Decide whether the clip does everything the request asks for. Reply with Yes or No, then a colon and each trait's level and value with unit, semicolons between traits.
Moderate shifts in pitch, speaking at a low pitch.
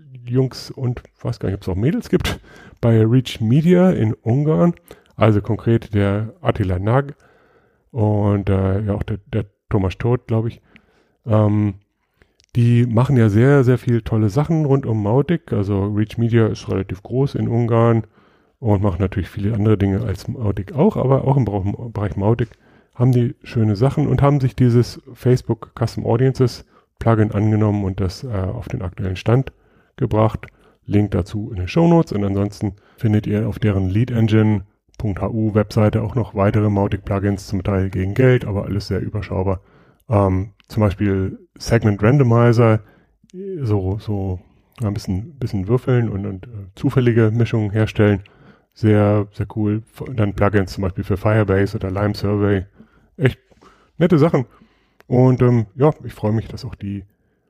Yes: average, 3.4 semitones; low, 110 Hz